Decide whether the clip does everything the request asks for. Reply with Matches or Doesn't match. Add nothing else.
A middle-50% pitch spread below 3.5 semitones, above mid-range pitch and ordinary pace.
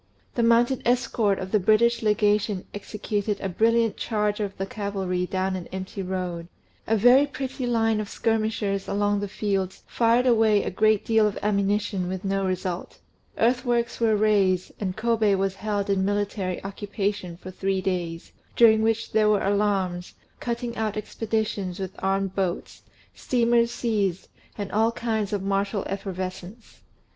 Matches